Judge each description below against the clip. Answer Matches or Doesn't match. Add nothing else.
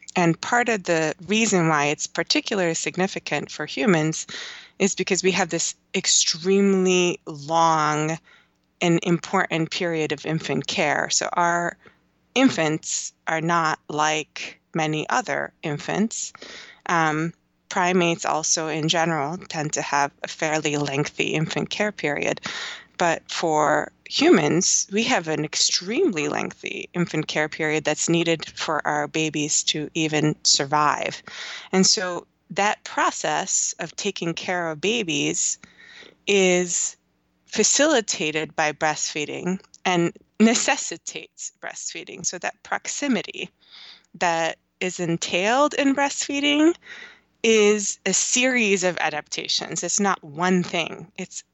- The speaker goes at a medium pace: Doesn't match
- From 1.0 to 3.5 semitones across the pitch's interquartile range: Doesn't match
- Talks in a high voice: Doesn't match